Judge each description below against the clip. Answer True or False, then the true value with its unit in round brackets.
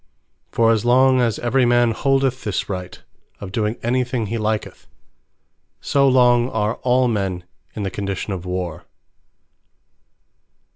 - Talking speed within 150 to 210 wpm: False (140 wpm)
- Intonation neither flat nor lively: True (3.9 semitones)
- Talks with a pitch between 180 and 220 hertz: False (115 Hz)